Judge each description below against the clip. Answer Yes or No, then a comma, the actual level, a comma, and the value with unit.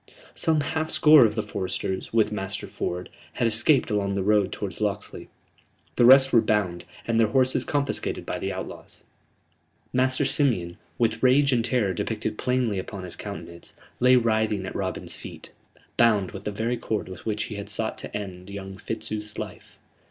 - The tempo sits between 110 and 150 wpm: No, average, 175 wpm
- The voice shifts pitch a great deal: No, average, 4.1 semitones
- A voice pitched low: Yes, low, 110 Hz